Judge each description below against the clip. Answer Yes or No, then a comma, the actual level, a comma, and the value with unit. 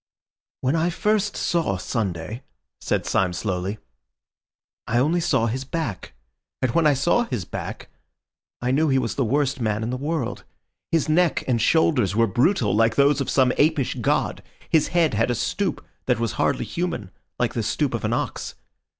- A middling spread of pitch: No, wide, 6.1 semitones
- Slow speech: No, average, 175 wpm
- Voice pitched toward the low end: Yes, low, 130 Hz